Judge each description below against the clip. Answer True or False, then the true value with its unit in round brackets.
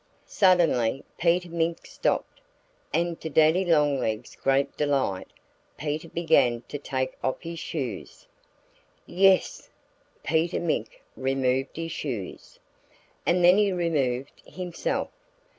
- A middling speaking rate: False (110 wpm)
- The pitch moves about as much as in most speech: True (4.4 semitones)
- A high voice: False (155 Hz)